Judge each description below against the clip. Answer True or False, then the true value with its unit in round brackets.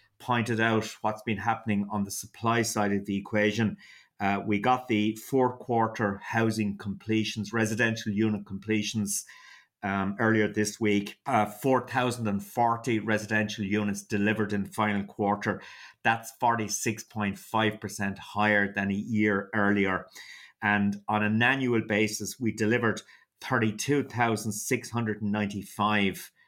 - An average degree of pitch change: False (1.8 semitones)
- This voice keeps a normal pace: False (115 wpm)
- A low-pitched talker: True (105 Hz)